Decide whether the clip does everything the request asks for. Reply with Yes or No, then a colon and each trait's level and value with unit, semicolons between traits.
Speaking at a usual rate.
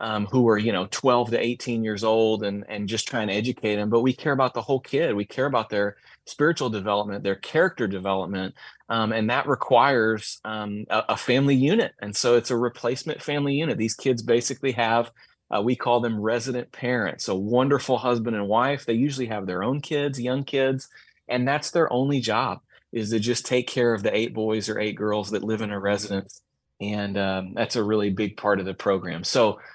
No: fast, 210 wpm